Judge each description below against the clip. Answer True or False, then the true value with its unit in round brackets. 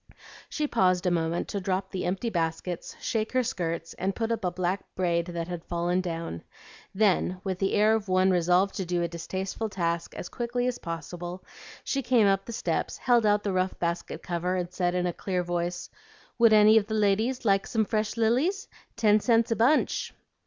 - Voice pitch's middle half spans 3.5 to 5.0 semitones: True (3.9 semitones)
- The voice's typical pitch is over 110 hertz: True (190 Hz)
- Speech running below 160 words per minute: False (200 wpm)